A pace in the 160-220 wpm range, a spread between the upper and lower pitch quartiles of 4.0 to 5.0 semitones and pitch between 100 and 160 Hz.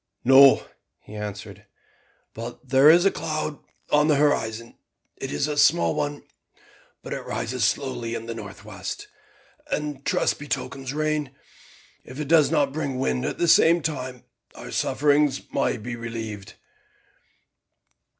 No: average, 145 wpm; average, 4.4 semitones; low, 135 Hz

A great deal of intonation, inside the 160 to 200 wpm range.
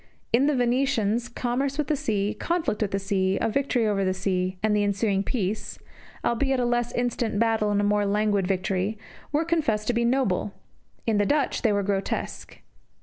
No: average, 3.5 semitones; average, 190 wpm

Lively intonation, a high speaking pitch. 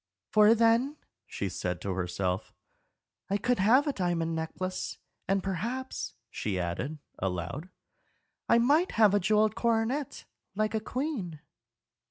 Yes: wide, 7.4 semitones; high, 200 Hz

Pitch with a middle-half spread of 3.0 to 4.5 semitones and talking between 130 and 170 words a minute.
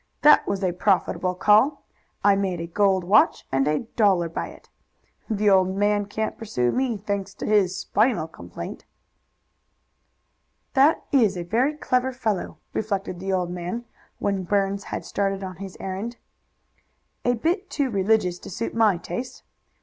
Yes: average, 3.3 semitones; average, 155 wpm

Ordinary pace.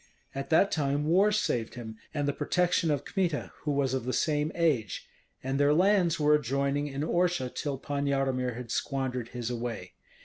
Yes: average, 180 wpm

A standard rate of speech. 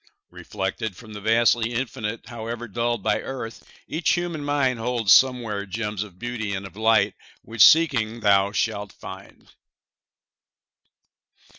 No: slow, 130 wpm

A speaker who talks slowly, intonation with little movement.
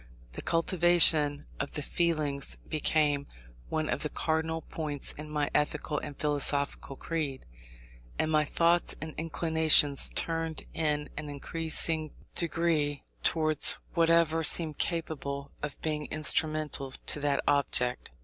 Yes: slow, 120 wpm; narrow, 1.9 semitones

